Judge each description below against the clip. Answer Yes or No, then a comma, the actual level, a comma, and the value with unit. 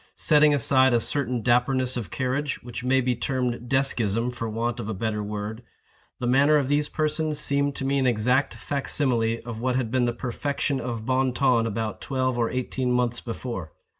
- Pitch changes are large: No, average, 2.7 semitones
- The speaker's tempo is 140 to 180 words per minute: No, average, 195 wpm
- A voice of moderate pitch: No, low, 125 Hz